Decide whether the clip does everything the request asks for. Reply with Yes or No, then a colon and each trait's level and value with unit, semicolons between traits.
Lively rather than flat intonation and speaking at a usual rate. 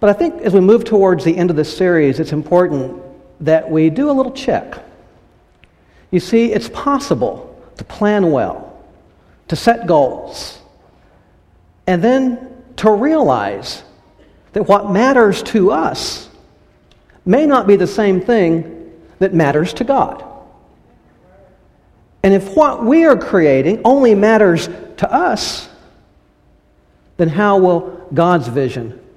No: wide, 6.3 semitones; slow, 130 wpm